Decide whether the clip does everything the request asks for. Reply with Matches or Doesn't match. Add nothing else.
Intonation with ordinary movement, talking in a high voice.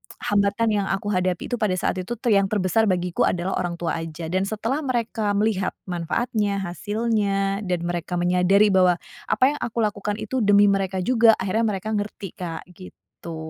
Matches